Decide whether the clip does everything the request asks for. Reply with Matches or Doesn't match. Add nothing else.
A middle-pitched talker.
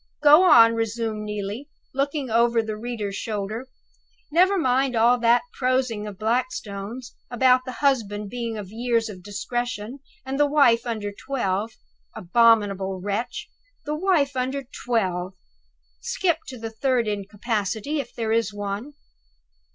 Doesn't match